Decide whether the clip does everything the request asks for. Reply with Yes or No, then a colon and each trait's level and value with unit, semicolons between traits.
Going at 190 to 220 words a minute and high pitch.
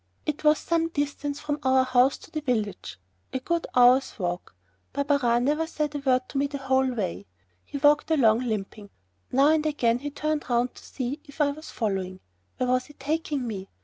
Yes: average, 195 wpm; very high, 270 Hz